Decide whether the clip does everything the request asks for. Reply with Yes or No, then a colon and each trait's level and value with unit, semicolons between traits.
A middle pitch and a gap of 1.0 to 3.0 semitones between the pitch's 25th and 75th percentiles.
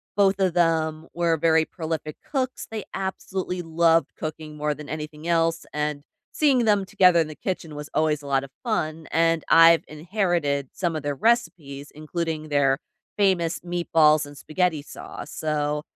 Yes: medium, 160 Hz; average, 2.7 semitones